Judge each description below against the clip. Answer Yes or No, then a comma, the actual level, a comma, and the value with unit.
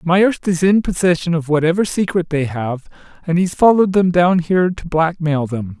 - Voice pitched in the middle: Yes, medium, 170 Hz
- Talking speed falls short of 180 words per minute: No, average, 185 wpm